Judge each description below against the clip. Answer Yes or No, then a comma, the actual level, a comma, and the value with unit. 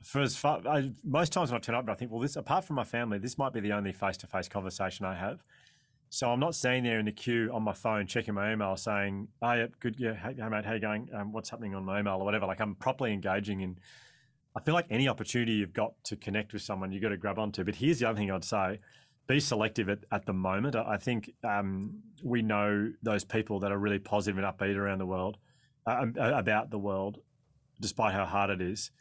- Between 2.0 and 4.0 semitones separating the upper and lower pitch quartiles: Yes, average, 3.5 semitones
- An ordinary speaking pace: No, fast, 245 wpm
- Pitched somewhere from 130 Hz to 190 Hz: No, low, 110 Hz